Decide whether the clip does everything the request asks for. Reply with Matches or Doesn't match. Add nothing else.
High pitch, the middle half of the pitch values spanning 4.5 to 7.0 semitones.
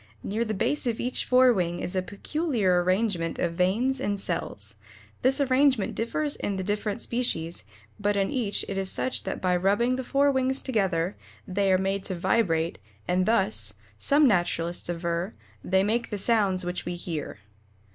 Matches